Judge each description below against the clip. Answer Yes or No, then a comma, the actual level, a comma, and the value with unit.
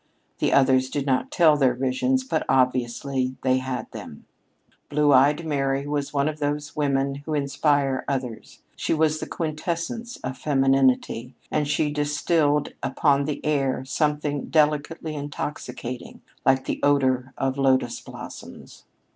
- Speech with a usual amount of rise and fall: No, narrow, 2.1 semitones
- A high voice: No, medium, 140 Hz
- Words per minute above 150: No, average, 140 wpm